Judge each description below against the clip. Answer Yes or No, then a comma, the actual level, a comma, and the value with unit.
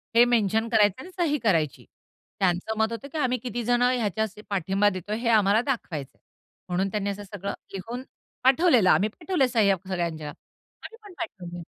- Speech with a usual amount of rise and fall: Yes, average, 4.3 semitones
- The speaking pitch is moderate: No, high, 215 Hz